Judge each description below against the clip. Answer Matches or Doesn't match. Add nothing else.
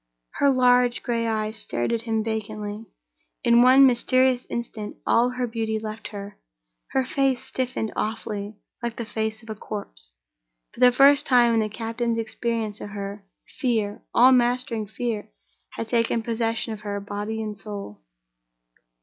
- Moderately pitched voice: Doesn't match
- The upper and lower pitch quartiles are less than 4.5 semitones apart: Matches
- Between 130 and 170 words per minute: Matches